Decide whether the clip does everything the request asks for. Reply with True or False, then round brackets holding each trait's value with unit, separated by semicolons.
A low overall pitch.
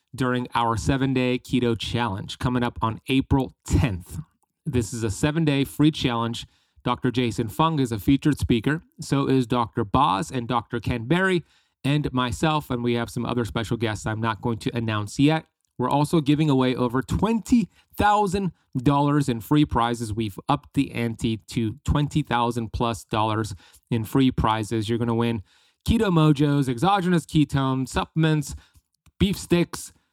True (125 Hz)